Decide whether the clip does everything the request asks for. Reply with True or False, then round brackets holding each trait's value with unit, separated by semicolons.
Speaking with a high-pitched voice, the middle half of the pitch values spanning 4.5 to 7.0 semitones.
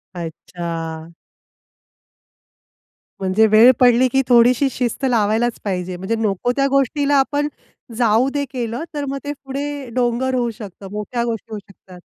True (235 Hz; 4.9 semitones)